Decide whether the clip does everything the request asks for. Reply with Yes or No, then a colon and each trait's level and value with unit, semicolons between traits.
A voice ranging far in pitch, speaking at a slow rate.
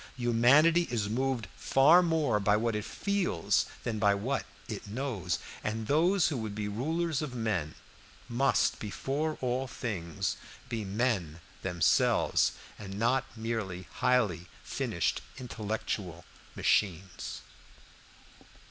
No: average, 4.8 semitones; slow, 115 wpm